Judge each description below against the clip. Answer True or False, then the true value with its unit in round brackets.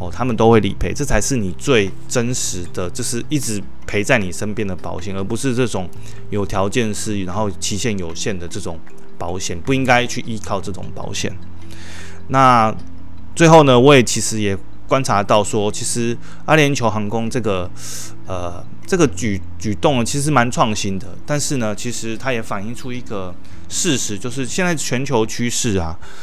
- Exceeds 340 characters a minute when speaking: False (260 characters per minute)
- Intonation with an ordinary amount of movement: True (4.6 semitones)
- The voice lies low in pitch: True (105 Hz)